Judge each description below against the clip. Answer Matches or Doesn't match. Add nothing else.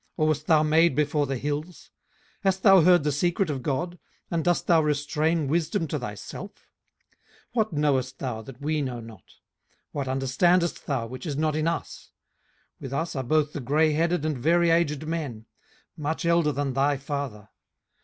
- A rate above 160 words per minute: Matches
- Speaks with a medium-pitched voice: Matches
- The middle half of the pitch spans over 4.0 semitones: Doesn't match